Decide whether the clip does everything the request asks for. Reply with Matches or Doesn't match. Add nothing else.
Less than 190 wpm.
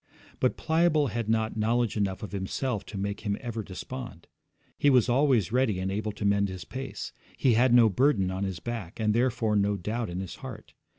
Doesn't match